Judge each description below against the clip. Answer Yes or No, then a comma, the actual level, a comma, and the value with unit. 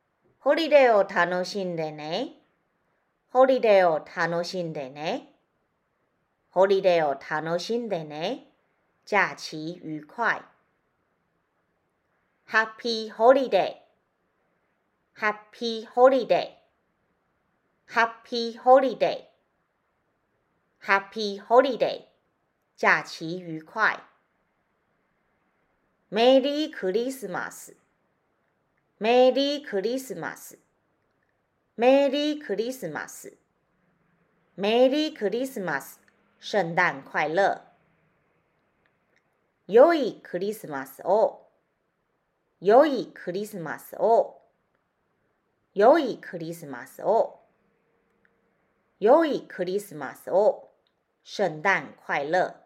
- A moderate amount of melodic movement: No, wide, 6.6 semitones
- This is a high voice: Yes, high, 210 Hz